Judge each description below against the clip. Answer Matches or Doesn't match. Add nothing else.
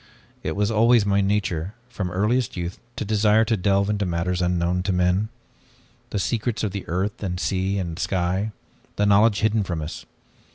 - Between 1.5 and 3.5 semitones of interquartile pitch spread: Matches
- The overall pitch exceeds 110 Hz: Doesn't match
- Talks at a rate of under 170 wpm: Doesn't match